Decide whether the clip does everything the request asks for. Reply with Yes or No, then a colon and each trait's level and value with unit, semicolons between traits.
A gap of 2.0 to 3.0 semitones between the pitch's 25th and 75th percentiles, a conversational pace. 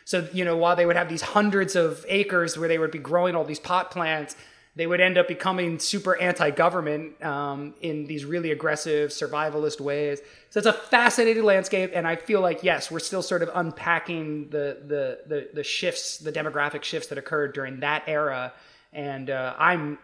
No: average, 3.4 semitones; average, 195 wpm